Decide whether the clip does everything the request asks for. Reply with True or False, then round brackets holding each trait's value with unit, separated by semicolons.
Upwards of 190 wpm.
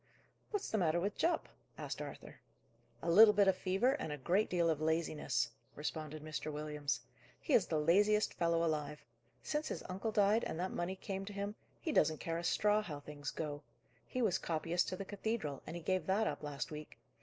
True (200 wpm)